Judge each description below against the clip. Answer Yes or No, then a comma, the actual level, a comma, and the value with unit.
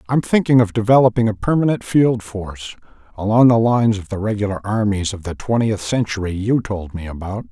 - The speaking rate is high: No, average, 185 wpm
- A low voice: Yes, low, 110 Hz